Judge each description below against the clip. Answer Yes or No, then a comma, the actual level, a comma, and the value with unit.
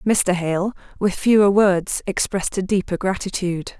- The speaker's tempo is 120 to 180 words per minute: Yes, average, 140 wpm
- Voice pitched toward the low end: No, high, 190 Hz